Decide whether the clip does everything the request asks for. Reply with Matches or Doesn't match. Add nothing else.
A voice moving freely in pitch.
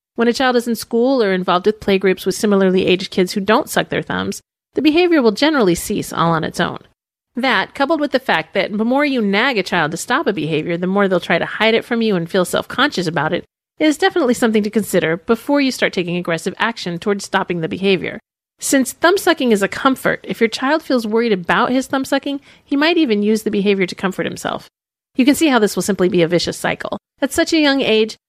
Matches